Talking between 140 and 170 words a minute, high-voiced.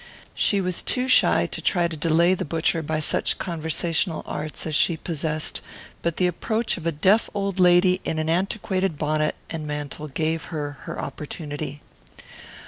No: average, 165 wpm; medium, 165 Hz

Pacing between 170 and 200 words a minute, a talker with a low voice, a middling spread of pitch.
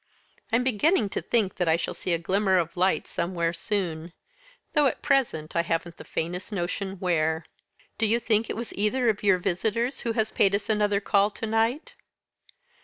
No: average, 185 wpm; high, 200 Hz; average, 4.4 semitones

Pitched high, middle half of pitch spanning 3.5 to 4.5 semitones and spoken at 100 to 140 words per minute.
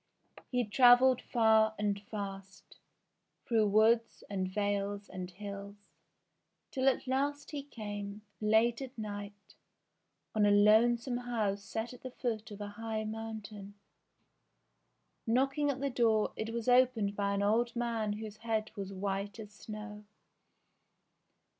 No: high, 215 Hz; average, 2.8 semitones; slow, 135 wpm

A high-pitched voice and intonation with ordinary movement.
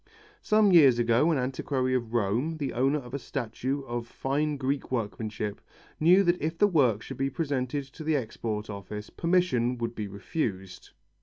No: low, 130 Hz; average, 4.6 semitones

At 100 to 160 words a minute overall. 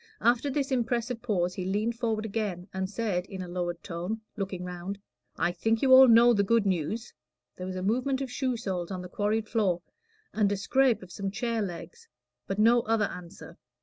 No: average, 200 wpm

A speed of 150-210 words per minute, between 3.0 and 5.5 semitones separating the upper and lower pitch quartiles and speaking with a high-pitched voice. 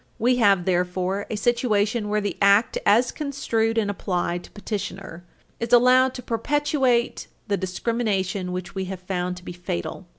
Yes: average, 160 wpm; average, 4.3 semitones; high, 205 Hz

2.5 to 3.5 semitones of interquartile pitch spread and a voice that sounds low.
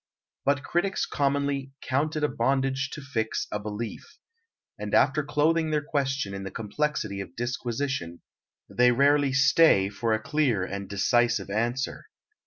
No: average, 4.7 semitones; low, 130 Hz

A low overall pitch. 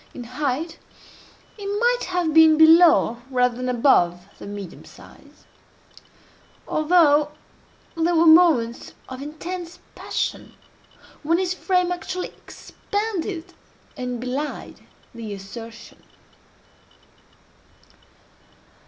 No: very high, 310 Hz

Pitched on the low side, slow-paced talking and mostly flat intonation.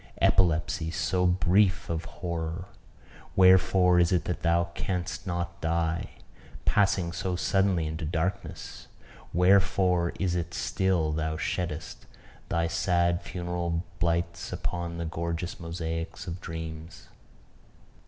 Yes: very low, 85 Hz; slow, 115 wpm; narrow, 1.6 semitones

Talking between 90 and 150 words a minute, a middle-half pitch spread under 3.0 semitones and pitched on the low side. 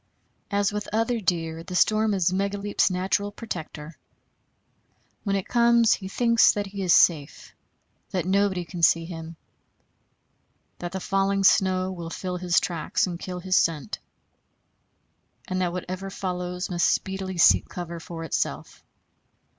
No: average, 140 wpm; narrow, 2.4 semitones; medium, 185 Hz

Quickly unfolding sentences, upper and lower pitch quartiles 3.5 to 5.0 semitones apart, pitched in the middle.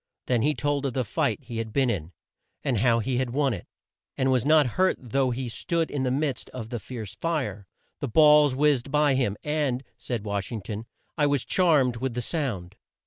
No: fast, 210 wpm; average, 3.9 semitones; low, 130 Hz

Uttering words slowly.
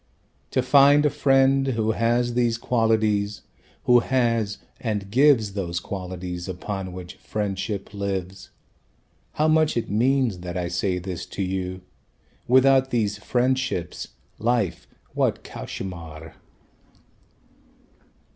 Yes: slow, 110 wpm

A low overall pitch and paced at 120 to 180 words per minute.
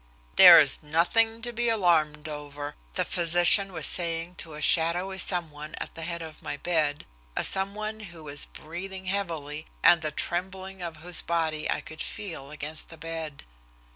No: medium, 165 Hz; average, 175 wpm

